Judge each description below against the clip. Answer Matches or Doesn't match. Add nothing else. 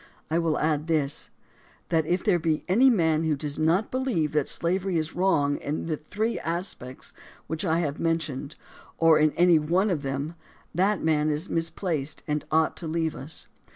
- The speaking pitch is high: Doesn't match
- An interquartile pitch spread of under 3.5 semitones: Matches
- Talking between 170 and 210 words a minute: Matches